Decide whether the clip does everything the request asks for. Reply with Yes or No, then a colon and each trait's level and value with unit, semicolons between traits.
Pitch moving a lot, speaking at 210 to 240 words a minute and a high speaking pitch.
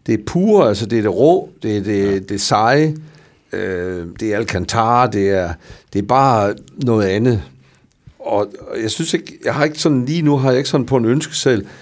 No: wide, 6.4 semitones; average, 220 wpm; low, 115 Hz